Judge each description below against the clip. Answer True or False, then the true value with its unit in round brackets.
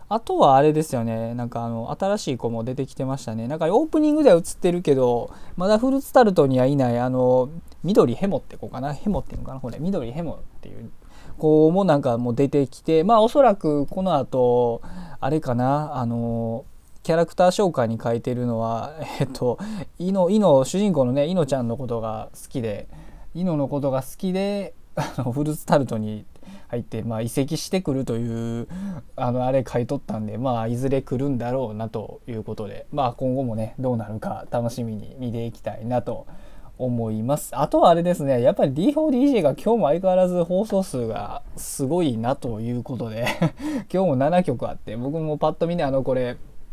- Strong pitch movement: True (6.0 semitones)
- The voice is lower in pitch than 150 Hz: True (135 Hz)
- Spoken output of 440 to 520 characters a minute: False (385 characters per minute)